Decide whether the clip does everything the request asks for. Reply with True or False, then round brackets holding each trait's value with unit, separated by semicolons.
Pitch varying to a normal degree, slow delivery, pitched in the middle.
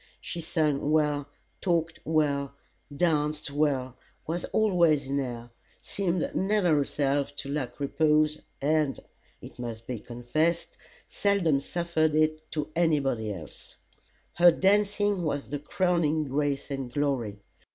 True (3.2 semitones; 125 wpm; 150 Hz)